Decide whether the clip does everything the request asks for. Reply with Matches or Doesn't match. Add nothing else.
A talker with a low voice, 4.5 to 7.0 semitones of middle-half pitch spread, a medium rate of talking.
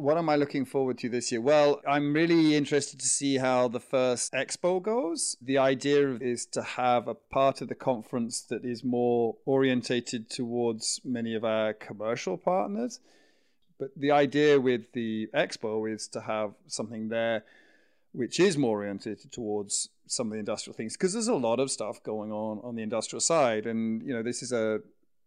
Doesn't match